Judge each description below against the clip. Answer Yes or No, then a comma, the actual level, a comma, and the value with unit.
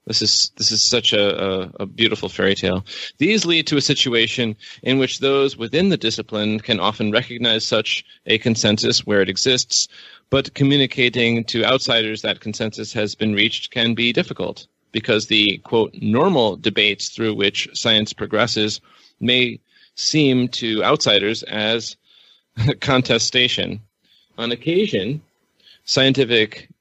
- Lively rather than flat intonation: No, average, 3.1 semitones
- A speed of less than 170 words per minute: Yes, slow, 135 wpm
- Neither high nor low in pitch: No, low, 115 Hz